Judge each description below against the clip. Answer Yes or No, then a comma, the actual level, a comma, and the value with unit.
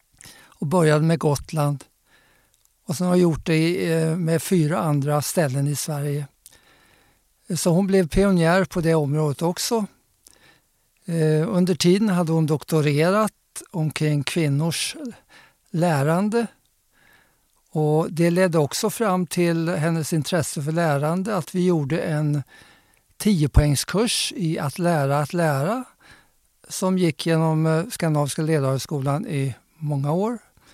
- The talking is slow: Yes, slow, 115 wpm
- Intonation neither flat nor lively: Yes, average, 3.1 semitones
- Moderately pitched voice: Yes, medium, 165 Hz